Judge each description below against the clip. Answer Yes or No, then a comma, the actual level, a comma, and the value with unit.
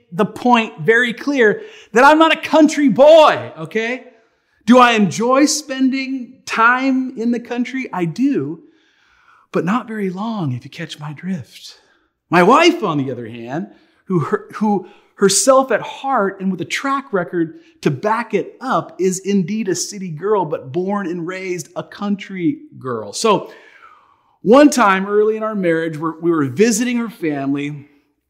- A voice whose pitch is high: Yes, high, 210 Hz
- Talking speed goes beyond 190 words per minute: No, average, 160 wpm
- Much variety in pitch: Yes, wide, 7.2 semitones